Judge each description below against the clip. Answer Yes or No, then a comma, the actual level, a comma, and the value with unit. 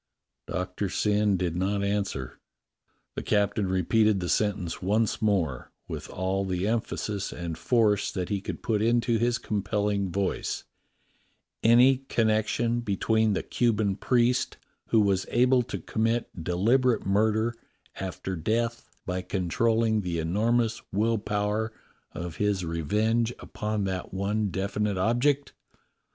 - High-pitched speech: No, low, 105 Hz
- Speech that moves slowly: Yes, slow, 130 wpm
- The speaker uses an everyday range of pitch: Yes, average, 3.1 semitones